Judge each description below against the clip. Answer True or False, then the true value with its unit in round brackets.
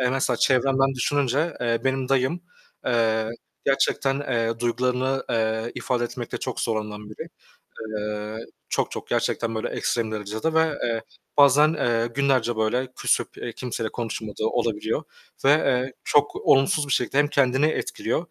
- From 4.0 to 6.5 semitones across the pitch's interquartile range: False (3.2 semitones)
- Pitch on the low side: True (125 Hz)